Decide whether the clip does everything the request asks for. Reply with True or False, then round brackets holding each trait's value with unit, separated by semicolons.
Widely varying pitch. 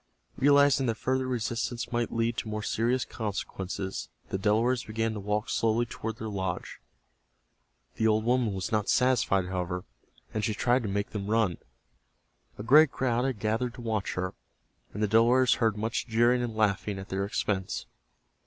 False (2.9 semitones)